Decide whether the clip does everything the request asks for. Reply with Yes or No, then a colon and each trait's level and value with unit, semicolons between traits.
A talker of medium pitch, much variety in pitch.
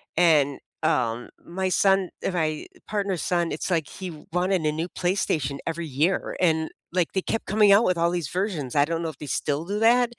No: medium, 170 Hz; average, 3.6 semitones